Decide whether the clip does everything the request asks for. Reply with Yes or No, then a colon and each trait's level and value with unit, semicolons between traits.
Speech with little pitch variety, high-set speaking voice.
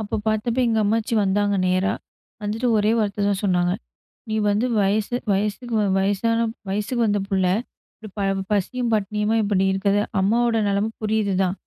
Yes: narrow, 2.0 semitones; high, 205 Hz